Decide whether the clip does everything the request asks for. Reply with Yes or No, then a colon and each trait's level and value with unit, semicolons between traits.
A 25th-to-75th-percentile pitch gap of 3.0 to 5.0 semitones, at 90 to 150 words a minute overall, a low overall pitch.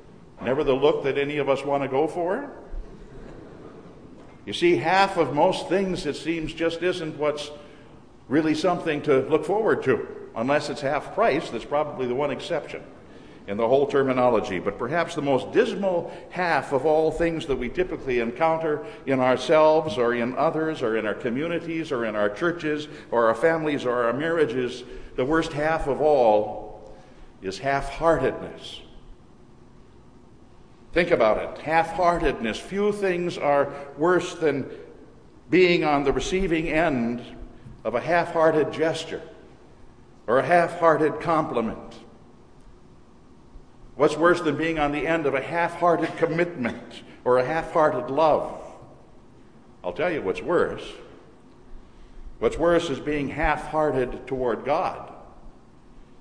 No: average, 4.3 semitones; average, 145 wpm; medium, 155 Hz